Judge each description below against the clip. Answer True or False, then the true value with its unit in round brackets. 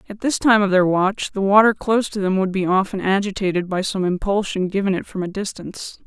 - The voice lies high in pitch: True (195 Hz)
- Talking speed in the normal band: False (225 wpm)